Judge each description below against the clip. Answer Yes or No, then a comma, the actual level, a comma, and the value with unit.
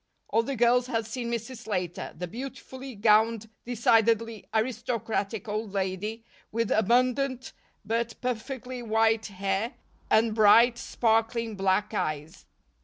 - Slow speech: Yes, slow, 115 wpm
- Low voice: No, high, 225 Hz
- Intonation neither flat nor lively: No, narrow, 2.2 semitones